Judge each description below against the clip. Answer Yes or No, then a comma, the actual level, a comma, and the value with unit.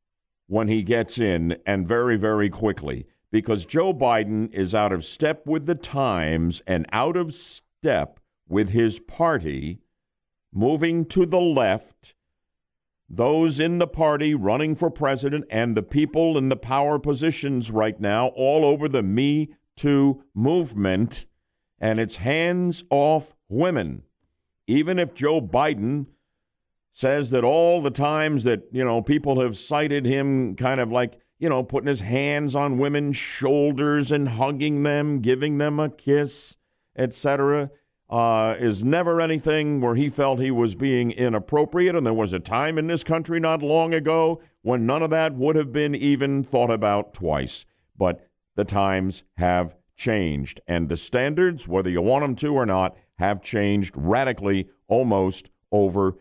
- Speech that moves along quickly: No, average, 155 wpm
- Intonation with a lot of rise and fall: Yes, wide, 5.7 semitones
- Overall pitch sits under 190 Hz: Yes, low, 135 Hz